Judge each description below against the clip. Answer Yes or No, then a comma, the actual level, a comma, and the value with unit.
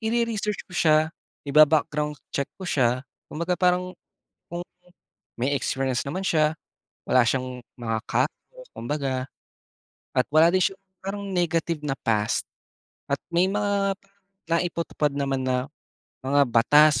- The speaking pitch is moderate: Yes, medium, 150 Hz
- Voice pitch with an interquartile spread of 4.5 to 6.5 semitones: Yes, average, 5.2 semitones